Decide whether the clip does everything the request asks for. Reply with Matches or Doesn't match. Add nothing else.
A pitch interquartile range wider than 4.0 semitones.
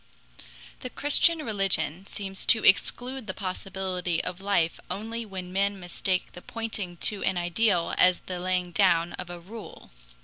Doesn't match